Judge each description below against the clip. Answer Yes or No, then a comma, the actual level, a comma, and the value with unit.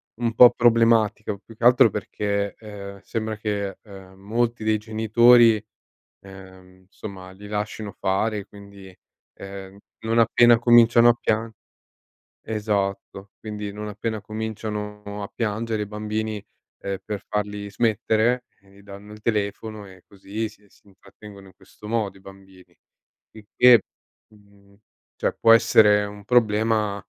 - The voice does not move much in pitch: Yes, narrow, 1.9 semitones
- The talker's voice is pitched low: Yes, low, 105 Hz